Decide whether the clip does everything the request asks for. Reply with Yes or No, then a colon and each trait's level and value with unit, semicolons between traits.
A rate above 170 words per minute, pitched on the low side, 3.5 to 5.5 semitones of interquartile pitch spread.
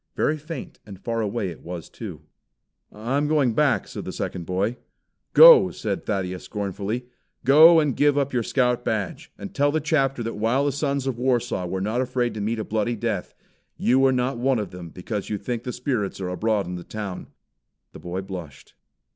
Yes: average, 195 wpm; low, 115 Hz; average, 5.1 semitones